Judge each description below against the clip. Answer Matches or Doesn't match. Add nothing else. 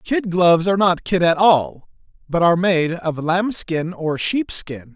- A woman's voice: Doesn't match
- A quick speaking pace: Doesn't match